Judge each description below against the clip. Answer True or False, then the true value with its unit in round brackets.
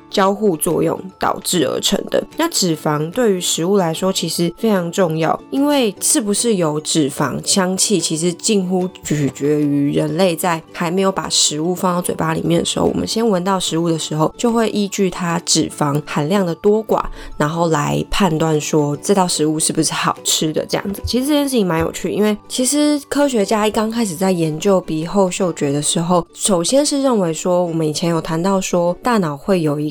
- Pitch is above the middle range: False (180 Hz)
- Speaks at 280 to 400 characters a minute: True (300 characters per minute)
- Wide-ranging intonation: False (4.2 semitones)